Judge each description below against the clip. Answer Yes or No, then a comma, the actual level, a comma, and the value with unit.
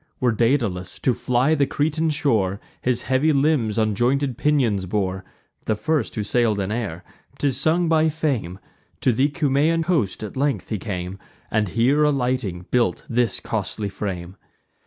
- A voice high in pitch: No, low, 120 Hz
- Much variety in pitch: Yes, wide, 5.8 semitones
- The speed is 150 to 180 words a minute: Yes, average, 155 wpm